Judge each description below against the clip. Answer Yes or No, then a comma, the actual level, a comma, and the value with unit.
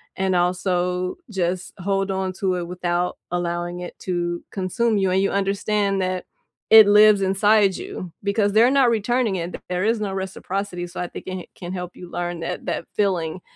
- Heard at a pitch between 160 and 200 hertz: Yes, medium, 185 Hz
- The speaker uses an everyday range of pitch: No, narrow, 2.2 semitones